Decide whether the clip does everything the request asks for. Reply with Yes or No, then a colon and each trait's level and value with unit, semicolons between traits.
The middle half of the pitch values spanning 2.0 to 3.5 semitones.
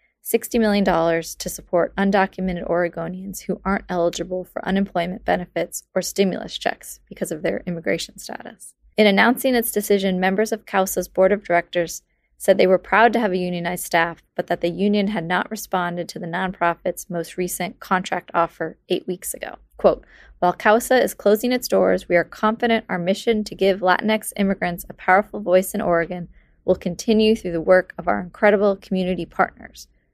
Yes: average, 2.9 semitones